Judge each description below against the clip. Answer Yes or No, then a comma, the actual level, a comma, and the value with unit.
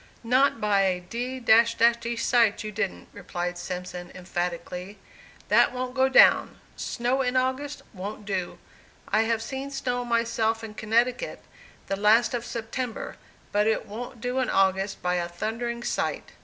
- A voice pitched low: No, high, 225 Hz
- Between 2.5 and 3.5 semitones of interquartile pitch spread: No, average, 4.0 semitones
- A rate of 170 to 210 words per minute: No, average, 150 wpm